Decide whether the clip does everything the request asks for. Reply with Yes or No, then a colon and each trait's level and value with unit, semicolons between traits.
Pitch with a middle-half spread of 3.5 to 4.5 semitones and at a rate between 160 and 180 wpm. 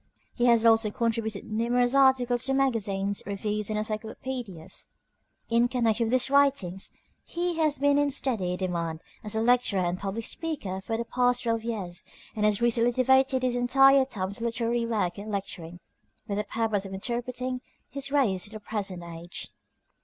Yes: average, 4.0 semitones; average, 170 wpm